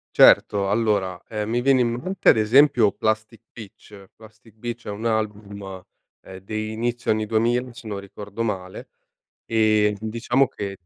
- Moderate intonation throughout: No, narrow, 2.2 semitones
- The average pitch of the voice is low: Yes, low, 110 Hz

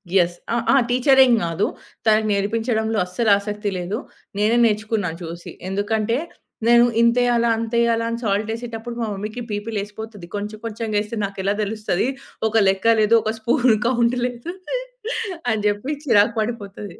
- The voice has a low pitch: No, high, 220 Hz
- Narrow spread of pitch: Yes, narrow, 2.3 semitones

